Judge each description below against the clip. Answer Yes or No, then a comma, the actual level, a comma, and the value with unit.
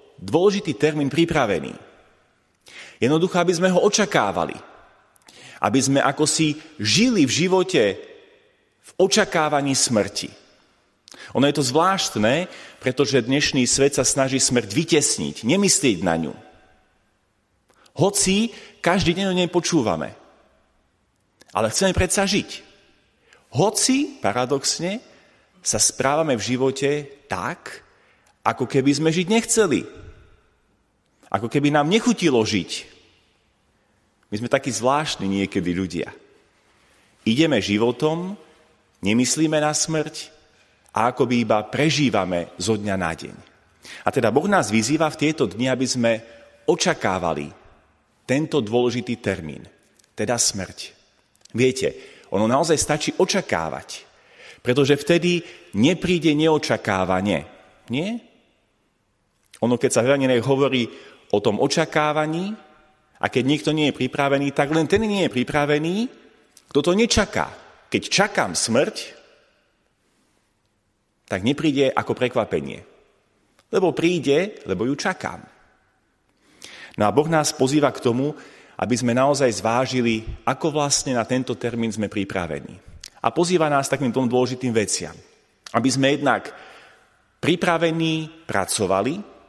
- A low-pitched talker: No, medium, 145 Hz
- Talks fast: No, average, 115 wpm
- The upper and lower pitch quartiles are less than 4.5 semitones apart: No, wide, 6.0 semitones